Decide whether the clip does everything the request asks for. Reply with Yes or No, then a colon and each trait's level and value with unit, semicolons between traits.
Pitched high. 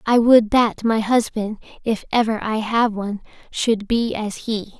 Yes: high, 220 Hz